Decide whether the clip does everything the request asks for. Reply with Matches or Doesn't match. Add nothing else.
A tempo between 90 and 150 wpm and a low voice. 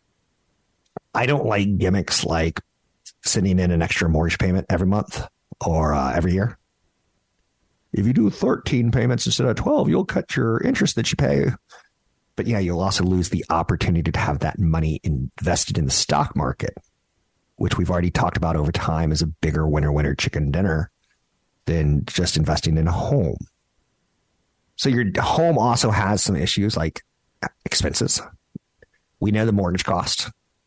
Doesn't match